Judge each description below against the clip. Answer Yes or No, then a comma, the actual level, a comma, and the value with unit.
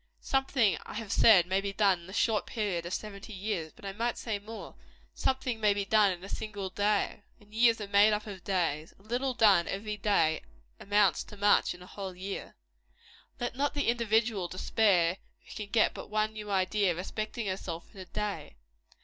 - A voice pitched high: Yes, high, 205 Hz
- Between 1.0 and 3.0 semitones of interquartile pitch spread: Yes, narrow, 2.5 semitones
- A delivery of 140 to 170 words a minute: No, average, 200 wpm